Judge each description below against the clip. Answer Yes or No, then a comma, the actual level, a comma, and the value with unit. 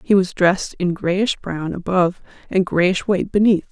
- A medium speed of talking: Yes, average, 180 wpm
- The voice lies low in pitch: No, medium, 185 Hz